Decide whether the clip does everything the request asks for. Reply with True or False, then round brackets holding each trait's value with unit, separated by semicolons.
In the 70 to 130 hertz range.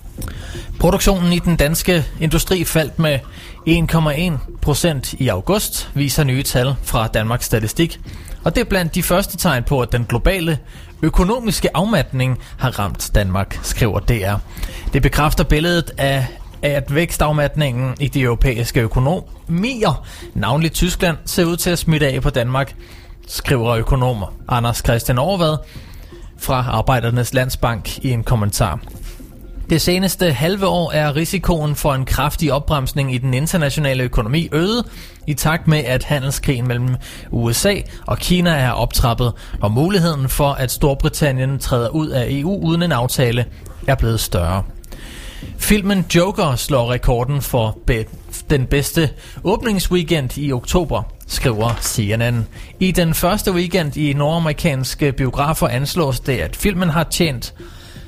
False (140 Hz)